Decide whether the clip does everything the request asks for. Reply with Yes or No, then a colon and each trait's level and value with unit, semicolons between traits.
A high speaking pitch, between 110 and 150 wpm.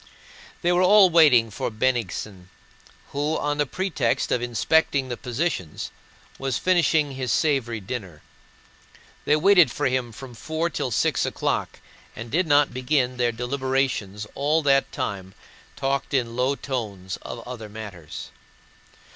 No: low, 130 Hz; average, 140 wpm